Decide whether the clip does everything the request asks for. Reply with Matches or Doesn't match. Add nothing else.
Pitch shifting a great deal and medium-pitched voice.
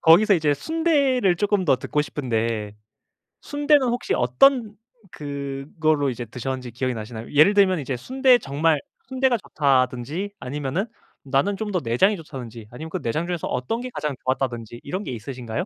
Matches